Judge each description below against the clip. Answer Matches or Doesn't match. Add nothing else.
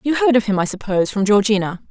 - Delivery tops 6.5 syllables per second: Matches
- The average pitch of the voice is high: Matches